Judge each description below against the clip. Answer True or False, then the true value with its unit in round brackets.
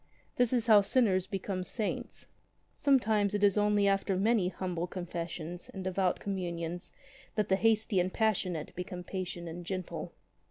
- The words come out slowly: False (155 wpm)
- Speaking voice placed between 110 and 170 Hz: False (190 Hz)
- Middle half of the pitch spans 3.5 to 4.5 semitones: False (2.7 semitones)